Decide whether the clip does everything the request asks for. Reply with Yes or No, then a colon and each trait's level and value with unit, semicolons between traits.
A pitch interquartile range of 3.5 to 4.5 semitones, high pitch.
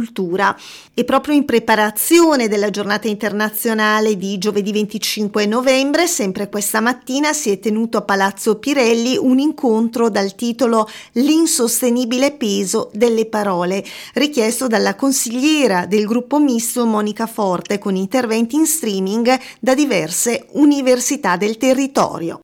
Yes: average, 3.8 semitones; high, 225 Hz